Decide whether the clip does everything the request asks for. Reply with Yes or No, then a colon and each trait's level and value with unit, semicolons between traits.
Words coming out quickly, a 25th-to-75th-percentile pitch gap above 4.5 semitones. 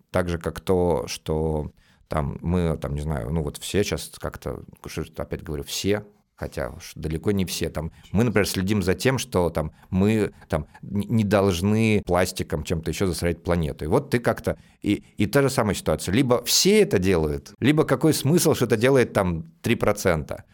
Yes: fast, 180 wpm; average, 4.9 semitones